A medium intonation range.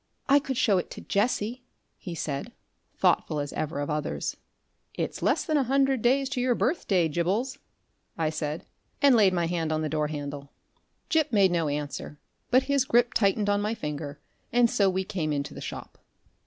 No: wide, 8.0 semitones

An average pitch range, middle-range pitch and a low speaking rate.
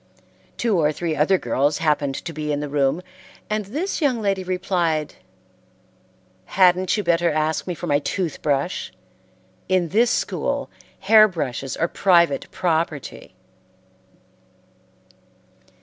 Yes: average, 4.0 semitones; medium, 170 Hz; slow, 125 wpm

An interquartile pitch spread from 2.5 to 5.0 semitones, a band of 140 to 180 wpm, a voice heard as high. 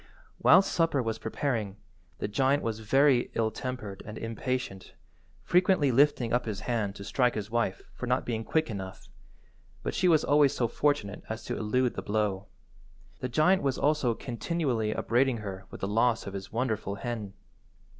No: average, 4.1 semitones; average, 165 wpm; low, 120 Hz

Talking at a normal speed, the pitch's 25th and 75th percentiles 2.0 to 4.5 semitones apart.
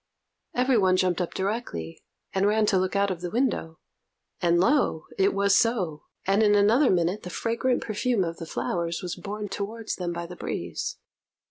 Yes: average, 185 wpm; average, 3.7 semitones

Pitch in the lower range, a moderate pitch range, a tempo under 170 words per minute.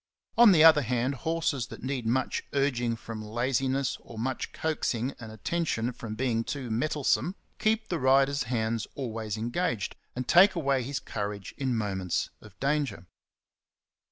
Yes: low, 130 Hz; average, 3.9 semitones; average, 155 wpm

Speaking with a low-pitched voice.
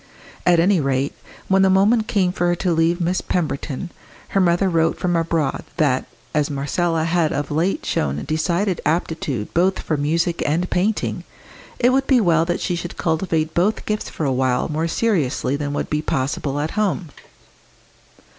No: medium, 165 Hz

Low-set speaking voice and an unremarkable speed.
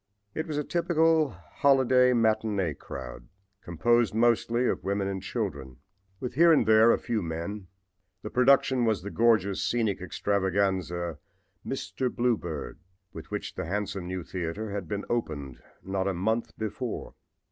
Yes: low, 105 Hz; average, 145 wpm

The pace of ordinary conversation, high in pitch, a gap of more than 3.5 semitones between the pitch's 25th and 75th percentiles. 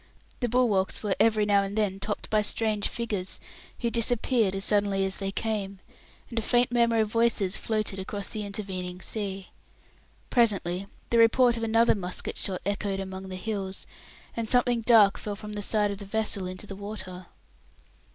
No: average, 175 wpm; high, 210 Hz; average, 2.7 semitones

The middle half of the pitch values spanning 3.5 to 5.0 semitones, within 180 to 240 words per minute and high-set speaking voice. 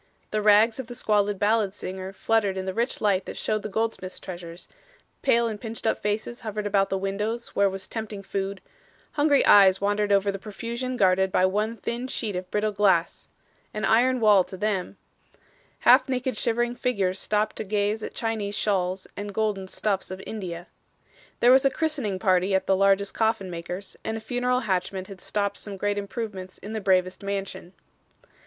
No: average, 2.7 semitones; average, 185 wpm; high, 205 Hz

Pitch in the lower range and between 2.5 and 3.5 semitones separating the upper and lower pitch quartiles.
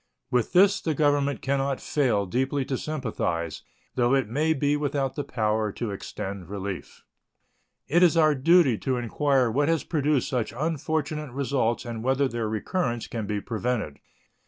No: low, 130 Hz; average, 4.5 semitones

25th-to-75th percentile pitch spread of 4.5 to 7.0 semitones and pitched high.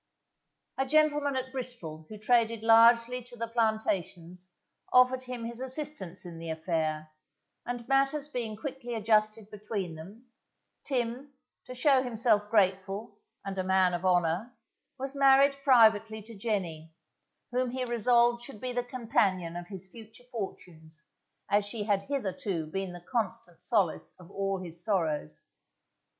Yes: average, 5.0 semitones; high, 220 Hz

